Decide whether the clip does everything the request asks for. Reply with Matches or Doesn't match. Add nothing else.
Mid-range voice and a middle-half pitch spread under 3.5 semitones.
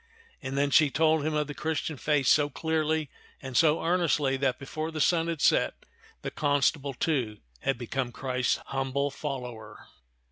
Matches